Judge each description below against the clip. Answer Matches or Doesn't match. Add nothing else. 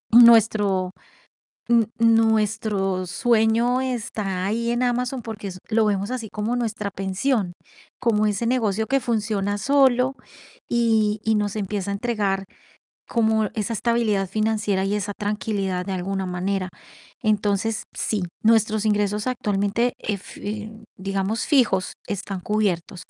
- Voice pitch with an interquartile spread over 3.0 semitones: Doesn't match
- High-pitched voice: Matches